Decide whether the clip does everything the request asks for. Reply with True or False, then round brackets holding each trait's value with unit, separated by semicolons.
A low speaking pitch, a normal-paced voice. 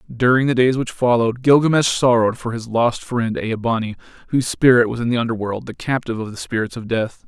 False (120 Hz; 215 wpm)